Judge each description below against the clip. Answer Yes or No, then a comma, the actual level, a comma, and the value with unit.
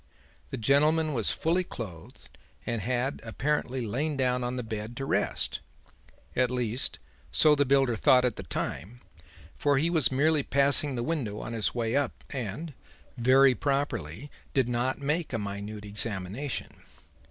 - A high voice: No, low, 125 Hz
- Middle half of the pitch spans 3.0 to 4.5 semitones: Yes, average, 3.9 semitones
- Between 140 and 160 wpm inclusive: Yes, average, 155 wpm